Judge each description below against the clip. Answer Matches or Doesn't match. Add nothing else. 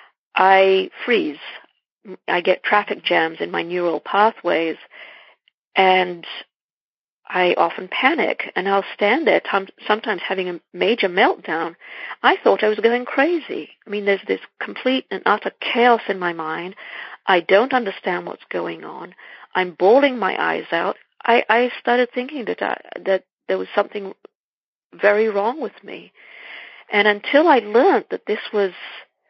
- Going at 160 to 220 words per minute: Doesn't match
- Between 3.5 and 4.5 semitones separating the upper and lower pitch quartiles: Matches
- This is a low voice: Doesn't match